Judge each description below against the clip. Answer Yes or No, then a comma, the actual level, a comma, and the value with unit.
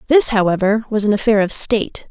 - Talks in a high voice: Yes, high, 215 Hz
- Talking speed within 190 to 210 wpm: Yes, average, 200 wpm